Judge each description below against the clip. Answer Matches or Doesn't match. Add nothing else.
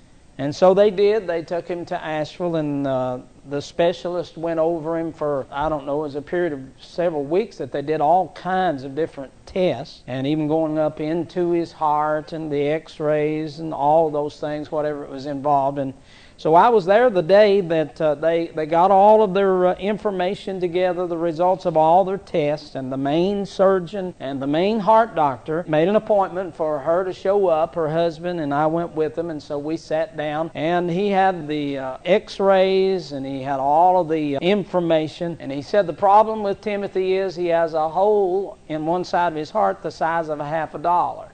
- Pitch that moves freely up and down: Doesn't match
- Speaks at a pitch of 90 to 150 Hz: Doesn't match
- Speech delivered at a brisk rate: Matches